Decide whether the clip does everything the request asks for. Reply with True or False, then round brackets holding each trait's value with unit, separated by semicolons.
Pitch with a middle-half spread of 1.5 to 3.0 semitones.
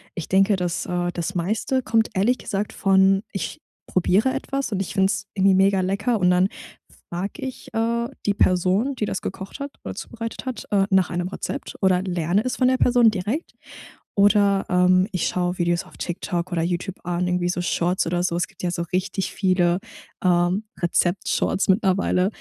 True (2.6 semitones)